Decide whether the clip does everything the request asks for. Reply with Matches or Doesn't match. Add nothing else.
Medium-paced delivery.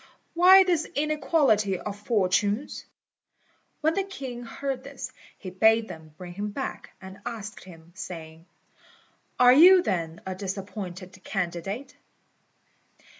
Doesn't match